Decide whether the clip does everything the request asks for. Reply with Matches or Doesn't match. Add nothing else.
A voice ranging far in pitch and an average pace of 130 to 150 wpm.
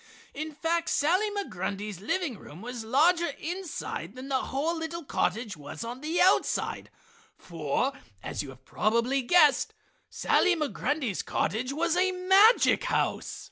Matches